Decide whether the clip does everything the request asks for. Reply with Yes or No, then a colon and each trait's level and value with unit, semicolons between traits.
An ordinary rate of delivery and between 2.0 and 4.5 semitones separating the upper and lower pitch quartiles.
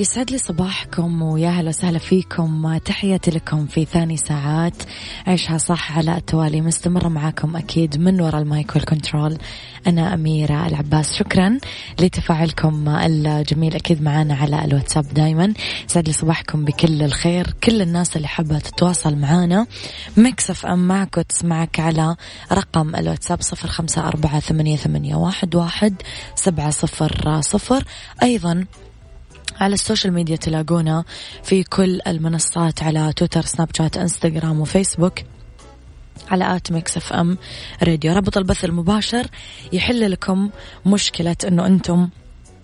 Yes: average, 125 wpm; average, 2.7 semitones